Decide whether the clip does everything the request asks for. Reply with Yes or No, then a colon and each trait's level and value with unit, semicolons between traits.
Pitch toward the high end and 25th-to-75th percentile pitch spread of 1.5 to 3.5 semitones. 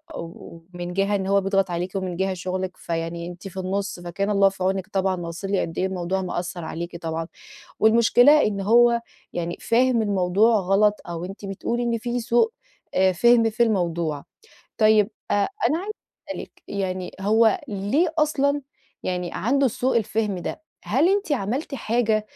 No: high, 195 Hz; average, 4.2 semitones